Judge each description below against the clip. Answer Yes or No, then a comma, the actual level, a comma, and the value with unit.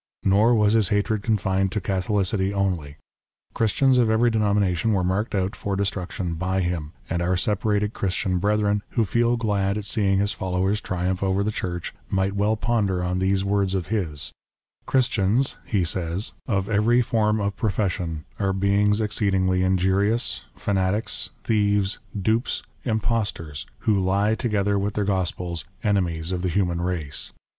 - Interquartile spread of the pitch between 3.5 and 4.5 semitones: No, narrow, 2.4 semitones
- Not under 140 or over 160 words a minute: Yes, average, 155 wpm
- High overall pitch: No, low, 100 Hz